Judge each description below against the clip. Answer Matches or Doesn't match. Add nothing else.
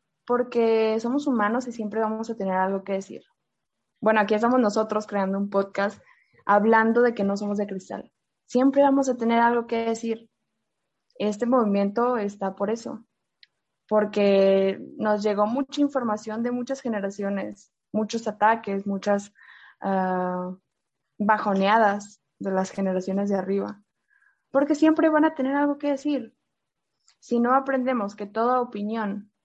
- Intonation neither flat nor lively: Matches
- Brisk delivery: Doesn't match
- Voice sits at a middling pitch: Doesn't match